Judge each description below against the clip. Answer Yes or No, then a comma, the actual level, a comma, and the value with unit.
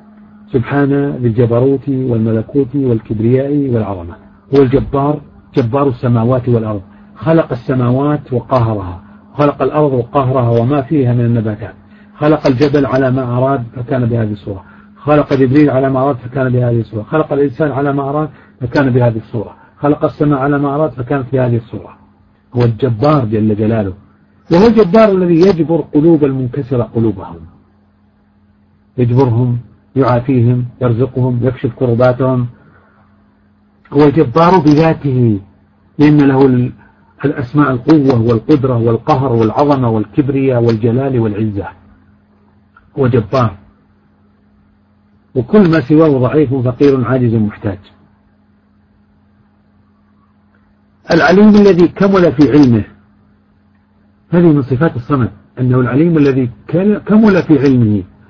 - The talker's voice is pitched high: No, low, 125 Hz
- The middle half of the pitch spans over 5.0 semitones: Yes, wide, 5.5 semitones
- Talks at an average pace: Yes, average, 110 wpm